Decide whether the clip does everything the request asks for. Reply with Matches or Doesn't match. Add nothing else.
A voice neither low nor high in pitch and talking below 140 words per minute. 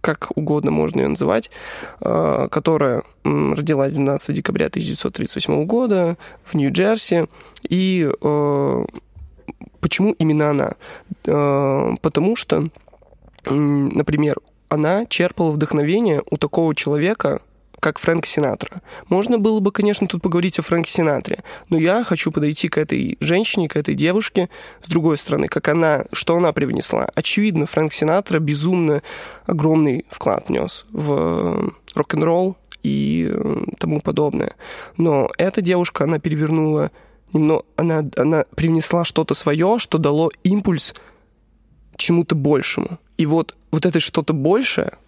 Matches